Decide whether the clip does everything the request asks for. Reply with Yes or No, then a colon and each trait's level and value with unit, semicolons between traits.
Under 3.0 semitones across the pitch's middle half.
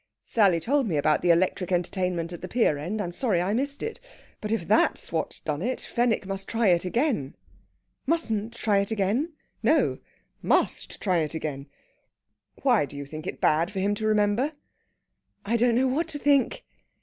No: wide, 5.6 semitones